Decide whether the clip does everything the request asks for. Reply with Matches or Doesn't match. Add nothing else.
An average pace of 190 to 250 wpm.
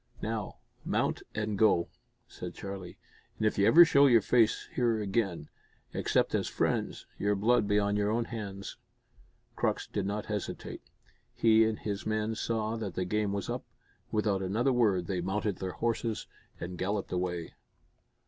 Doesn't match